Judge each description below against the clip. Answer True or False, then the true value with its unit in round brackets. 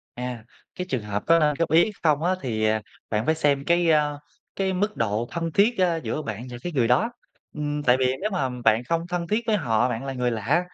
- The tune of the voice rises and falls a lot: True (6.0 semitones)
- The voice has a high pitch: False (150 Hz)